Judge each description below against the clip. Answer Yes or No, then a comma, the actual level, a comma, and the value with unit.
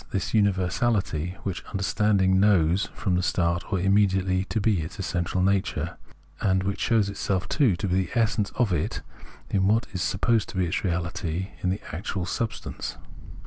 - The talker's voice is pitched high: No, very low, 95 Hz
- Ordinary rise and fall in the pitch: No, narrow, 2.2 semitones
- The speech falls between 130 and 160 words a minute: No, average, 170 wpm